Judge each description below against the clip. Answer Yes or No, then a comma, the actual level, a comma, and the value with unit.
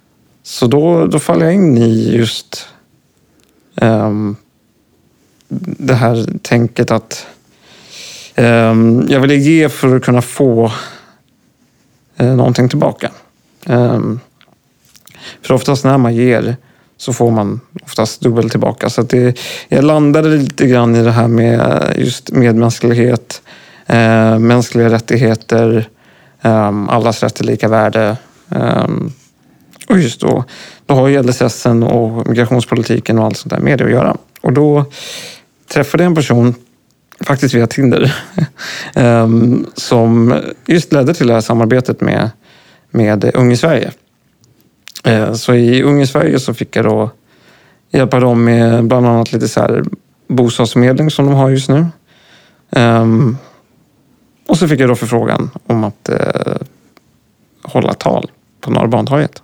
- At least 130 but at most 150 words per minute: Yes, average, 135 wpm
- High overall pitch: No, low, 120 Hz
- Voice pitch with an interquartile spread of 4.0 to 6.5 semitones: No, narrow, 2.6 semitones